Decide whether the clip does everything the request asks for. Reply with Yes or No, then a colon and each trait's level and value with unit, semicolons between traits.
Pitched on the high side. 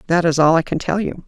No: medium, 170 Hz